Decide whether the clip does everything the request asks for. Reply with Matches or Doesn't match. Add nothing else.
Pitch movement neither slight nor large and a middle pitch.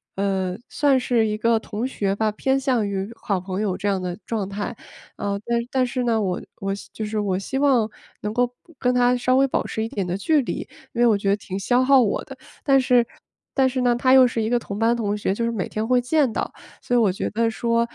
Doesn't match